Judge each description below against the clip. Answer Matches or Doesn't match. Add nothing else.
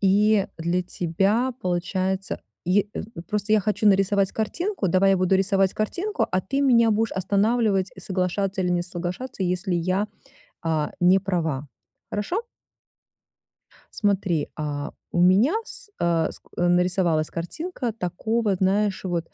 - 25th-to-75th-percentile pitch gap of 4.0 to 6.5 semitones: Doesn't match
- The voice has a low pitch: Doesn't match